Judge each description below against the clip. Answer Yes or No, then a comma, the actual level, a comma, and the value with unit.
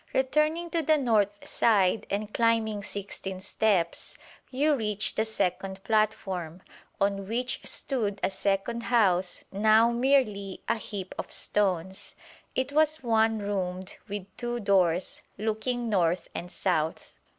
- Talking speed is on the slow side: Yes, slow, 130 wpm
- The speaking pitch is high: Yes, high, 210 Hz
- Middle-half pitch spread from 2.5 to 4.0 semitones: Yes, average, 3.6 semitones